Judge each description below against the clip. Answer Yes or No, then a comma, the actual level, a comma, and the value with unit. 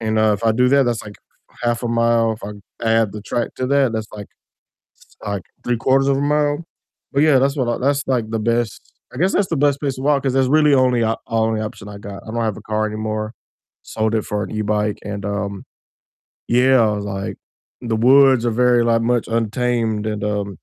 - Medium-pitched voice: No, low, 115 Hz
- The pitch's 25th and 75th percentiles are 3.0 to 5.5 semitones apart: Yes, average, 3.5 semitones